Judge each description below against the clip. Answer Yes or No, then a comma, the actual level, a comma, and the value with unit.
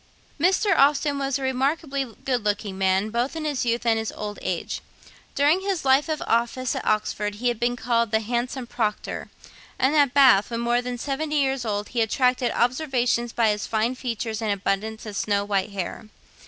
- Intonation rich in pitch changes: No, average, 4.0 semitones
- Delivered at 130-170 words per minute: No, average, 190 wpm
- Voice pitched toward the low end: No, high, 240 Hz